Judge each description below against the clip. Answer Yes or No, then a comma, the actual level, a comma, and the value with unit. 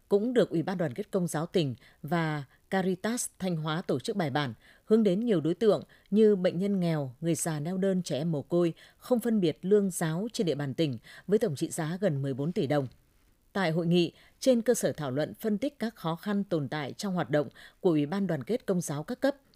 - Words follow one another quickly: No, average, 235 wpm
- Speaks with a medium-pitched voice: Yes, medium, 175 Hz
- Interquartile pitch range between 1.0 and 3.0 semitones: No, average, 4.9 semitones